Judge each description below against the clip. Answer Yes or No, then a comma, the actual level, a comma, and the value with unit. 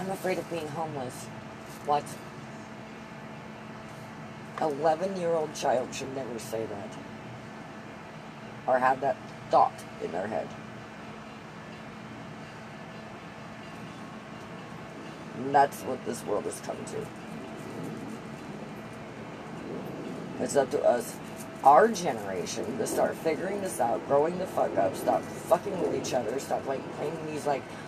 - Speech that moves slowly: Yes, slow, 115 wpm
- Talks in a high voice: No, low, 135 Hz